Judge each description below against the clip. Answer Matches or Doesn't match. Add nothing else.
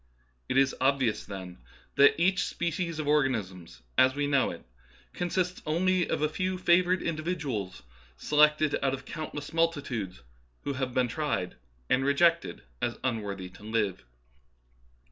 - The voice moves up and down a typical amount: Doesn't match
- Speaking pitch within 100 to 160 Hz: Matches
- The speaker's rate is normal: Matches